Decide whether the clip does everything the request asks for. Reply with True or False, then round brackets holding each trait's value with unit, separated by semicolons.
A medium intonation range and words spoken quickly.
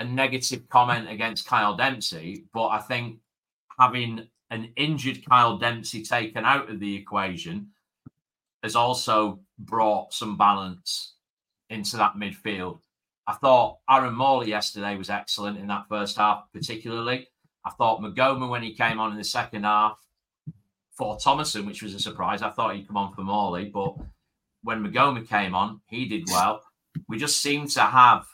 False (3.4 semitones; 160 wpm)